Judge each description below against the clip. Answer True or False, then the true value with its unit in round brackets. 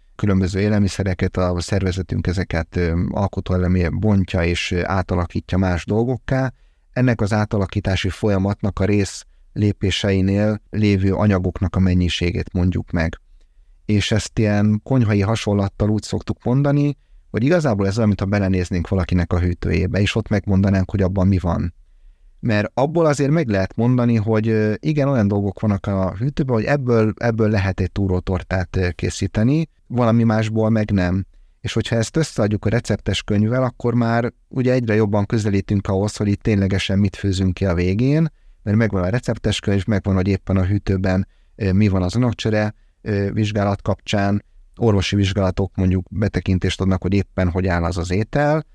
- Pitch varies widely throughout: False (2.9 semitones)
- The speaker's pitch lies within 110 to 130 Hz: False (100 Hz)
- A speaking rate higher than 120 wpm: True (150 wpm)